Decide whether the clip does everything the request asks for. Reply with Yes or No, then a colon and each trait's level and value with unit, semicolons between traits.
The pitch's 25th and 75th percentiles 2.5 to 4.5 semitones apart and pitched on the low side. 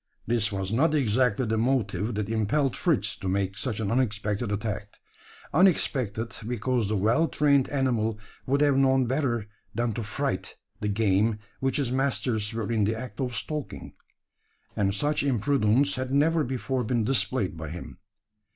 Yes: average, 4.1 semitones; low, 115 Hz